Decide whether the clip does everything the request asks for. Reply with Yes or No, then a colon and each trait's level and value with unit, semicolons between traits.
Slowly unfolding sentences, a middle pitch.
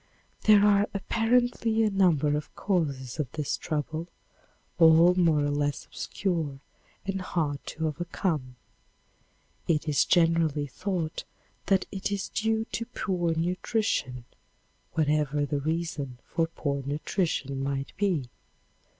Yes: slow, 120 wpm; medium, 165 Hz